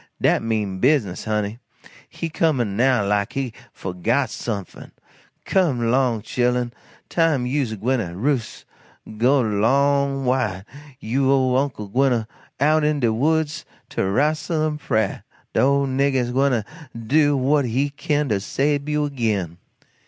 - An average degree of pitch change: Yes, average, 4.3 semitones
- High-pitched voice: No, low, 130 Hz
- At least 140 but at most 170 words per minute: Yes, average, 145 wpm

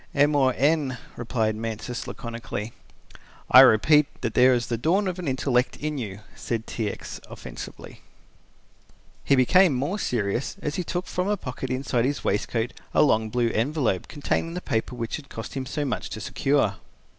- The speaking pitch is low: Yes, low, 130 Hz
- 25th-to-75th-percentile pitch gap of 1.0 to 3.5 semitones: No, average, 4.5 semitones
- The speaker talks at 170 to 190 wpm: Yes, average, 175 wpm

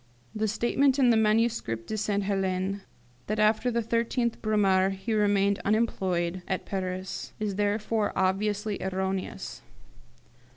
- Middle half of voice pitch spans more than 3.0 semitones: No, narrow, 2.4 semitones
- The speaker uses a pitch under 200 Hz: No, high, 205 Hz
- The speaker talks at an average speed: No, slow, 125 wpm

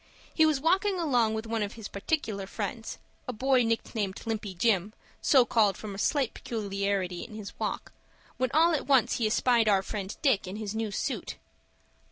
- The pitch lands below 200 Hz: No, high, 220 Hz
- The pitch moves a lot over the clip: No, average, 4.1 semitones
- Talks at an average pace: Yes, average, 185 wpm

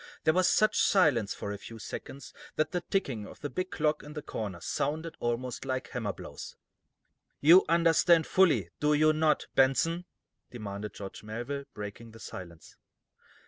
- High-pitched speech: No, medium, 140 Hz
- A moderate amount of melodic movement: No, wide, 6.5 semitones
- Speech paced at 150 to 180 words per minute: Yes, average, 160 wpm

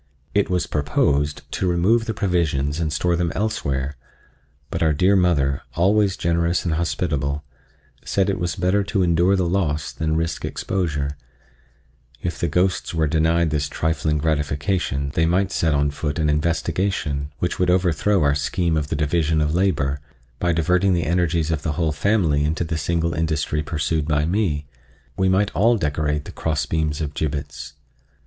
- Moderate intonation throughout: Yes, average, 3.3 semitones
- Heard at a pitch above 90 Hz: No, very low, 80 Hz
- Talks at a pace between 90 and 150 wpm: No, average, 165 wpm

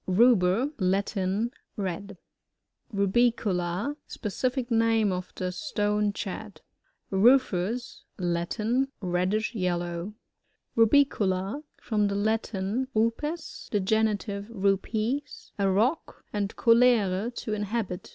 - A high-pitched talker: Yes, high, 210 Hz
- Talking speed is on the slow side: Yes, slow, 105 wpm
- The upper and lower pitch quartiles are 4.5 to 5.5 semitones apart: No, average, 3.5 semitones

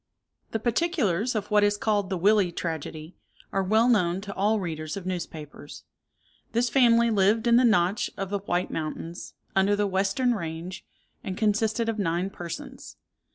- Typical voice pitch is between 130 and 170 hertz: No, high, 200 Hz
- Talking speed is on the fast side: No, average, 160 wpm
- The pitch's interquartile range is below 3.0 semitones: No, average, 4.0 semitones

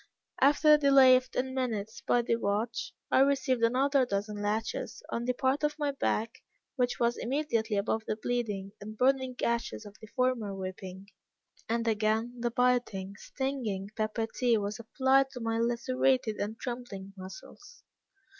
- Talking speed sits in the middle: Yes, average, 155 wpm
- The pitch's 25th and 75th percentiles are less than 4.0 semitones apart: Yes, average, 3.4 semitones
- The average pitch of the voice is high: Yes, high, 235 Hz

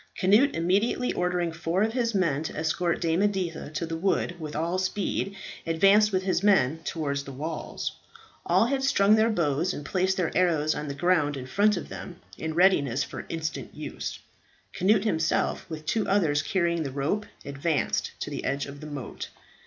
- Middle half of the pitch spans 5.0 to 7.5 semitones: No, average, 4.2 semitones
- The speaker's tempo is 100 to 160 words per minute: No, average, 185 wpm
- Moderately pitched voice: Yes, medium, 170 Hz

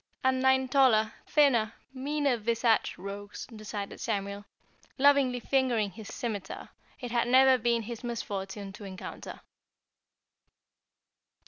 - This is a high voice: Yes, high, 235 Hz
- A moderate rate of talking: No, slow, 110 wpm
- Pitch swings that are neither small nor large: Yes, average, 4.1 semitones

